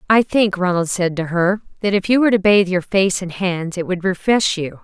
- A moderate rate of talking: No, fast, 250 wpm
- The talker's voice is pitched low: No, high, 190 Hz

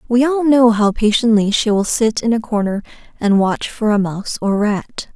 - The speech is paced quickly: Yes, fast, 210 wpm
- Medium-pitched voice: No, high, 220 Hz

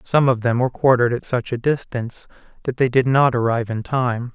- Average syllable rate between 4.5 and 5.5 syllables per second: No, 5.9 syllables/s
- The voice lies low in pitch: Yes, low, 125 Hz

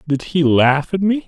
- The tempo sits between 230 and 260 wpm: Yes, fast, 235 wpm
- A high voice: No, medium, 165 Hz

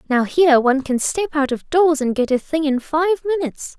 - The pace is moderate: No, fast, 240 wpm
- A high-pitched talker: Yes, very high, 300 Hz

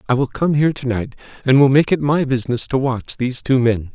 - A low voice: Yes, low, 130 Hz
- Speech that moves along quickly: Yes, fast, 260 wpm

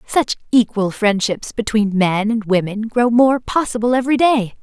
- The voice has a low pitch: No, high, 225 Hz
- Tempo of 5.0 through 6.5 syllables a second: No, 4.6 syllables/s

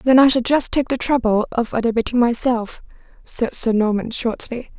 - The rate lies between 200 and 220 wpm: No, average, 175 wpm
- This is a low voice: No, high, 240 Hz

